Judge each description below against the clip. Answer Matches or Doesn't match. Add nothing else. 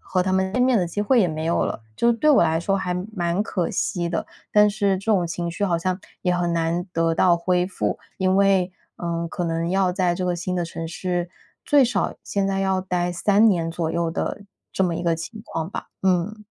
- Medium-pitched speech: Matches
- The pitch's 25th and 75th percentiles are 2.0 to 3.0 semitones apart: Matches